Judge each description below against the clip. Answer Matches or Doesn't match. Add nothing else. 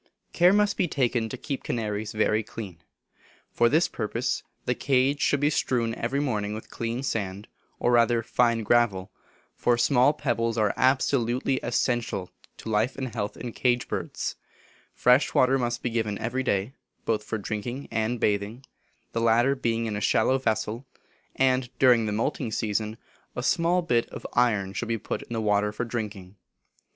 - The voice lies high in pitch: Doesn't match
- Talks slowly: Doesn't match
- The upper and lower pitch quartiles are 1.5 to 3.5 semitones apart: Matches